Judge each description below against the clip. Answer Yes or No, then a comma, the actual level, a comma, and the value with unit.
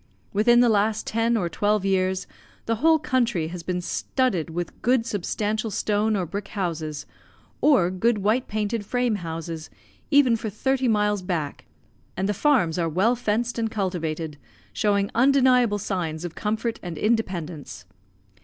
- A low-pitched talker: No, high, 210 Hz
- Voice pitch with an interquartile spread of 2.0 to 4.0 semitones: No, average, 4.7 semitones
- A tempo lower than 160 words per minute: Yes, average, 150 wpm